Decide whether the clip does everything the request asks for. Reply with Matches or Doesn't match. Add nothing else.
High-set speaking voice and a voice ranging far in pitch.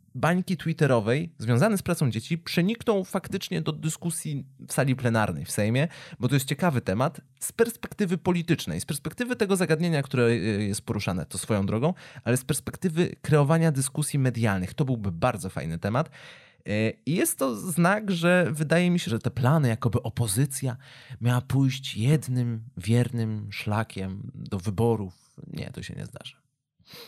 Doesn't match